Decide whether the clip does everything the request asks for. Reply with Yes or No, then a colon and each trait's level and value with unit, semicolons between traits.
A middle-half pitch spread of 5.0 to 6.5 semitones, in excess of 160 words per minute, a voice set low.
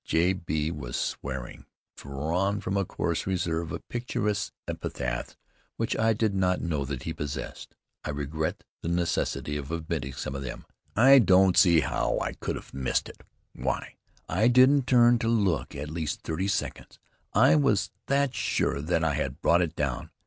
Yes: wide, 5.4 semitones; average, 175 wpm; very low, 85 Hz